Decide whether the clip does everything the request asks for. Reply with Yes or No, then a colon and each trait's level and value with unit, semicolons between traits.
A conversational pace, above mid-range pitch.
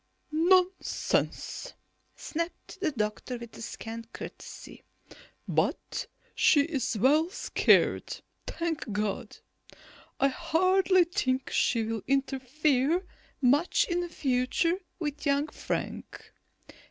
No: slow, 90 wpm; very high, 290 Hz